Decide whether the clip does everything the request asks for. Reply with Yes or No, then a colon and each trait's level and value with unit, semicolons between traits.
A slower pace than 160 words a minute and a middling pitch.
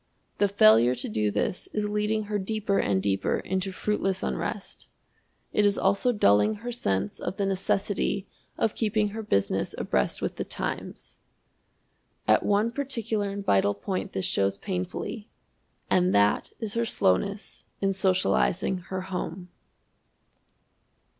No: average, 140 wpm; high, 195 Hz